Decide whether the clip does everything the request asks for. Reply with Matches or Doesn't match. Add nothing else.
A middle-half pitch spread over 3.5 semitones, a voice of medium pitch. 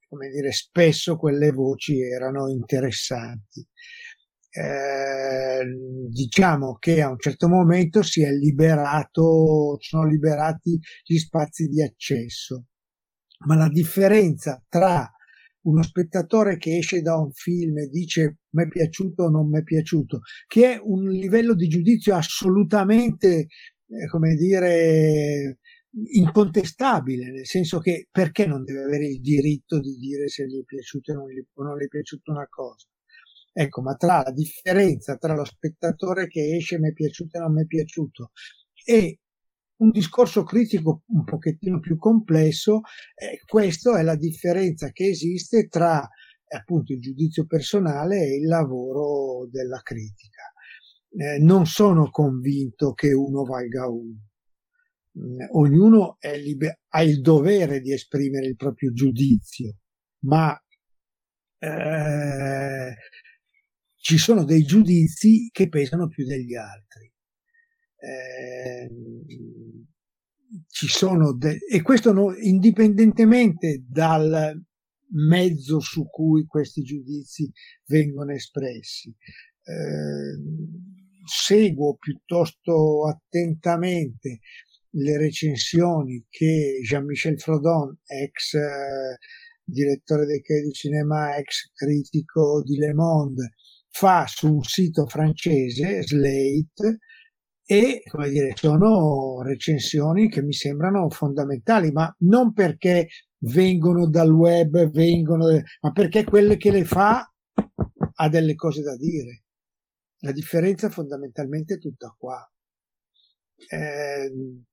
Matches